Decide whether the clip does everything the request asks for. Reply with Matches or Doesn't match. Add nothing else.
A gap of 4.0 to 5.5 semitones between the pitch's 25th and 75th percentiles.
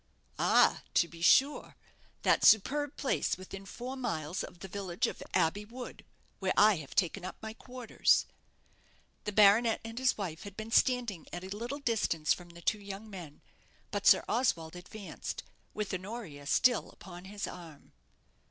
Matches